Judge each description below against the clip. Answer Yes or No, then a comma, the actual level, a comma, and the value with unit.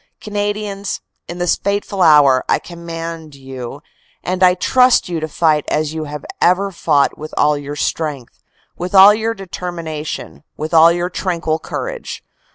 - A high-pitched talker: No, medium, 170 Hz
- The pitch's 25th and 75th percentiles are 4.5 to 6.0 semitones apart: No, average, 4.0 semitones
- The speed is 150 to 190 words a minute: Yes, average, 155 wpm